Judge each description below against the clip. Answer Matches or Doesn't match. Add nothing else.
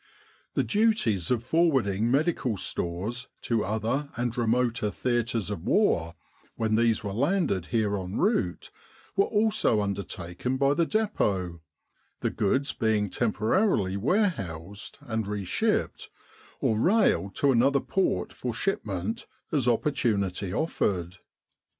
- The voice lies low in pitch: Matches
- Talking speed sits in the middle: Doesn't match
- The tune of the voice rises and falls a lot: Matches